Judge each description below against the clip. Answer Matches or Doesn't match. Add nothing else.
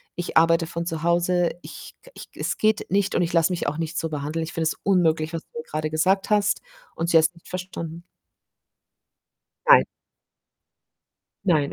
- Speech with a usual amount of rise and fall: Doesn't match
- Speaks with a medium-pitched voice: Matches